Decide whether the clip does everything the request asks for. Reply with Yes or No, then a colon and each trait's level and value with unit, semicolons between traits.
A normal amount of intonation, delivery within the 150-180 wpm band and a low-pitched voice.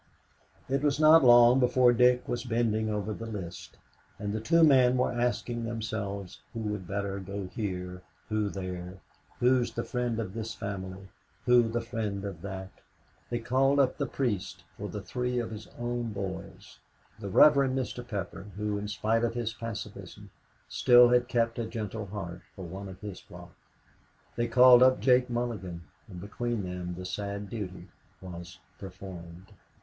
Yes: average, 3.9 semitones; average, 165 wpm; low, 110 Hz